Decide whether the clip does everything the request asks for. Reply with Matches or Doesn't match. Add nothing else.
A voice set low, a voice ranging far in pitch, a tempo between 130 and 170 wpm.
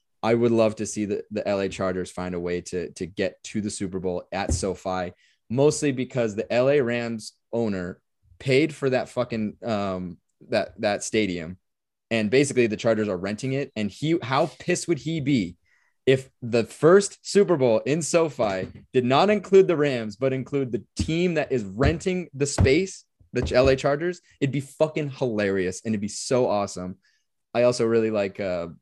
Doesn't match